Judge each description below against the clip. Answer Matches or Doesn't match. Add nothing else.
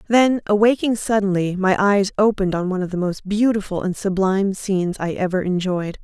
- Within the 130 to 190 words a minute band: Matches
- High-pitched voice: Matches